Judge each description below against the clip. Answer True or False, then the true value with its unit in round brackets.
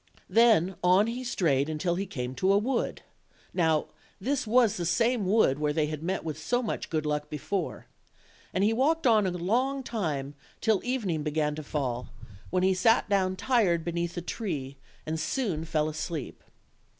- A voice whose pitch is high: False (180 Hz)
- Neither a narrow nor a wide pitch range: False (6.4 semitones)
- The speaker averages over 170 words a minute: True (180 wpm)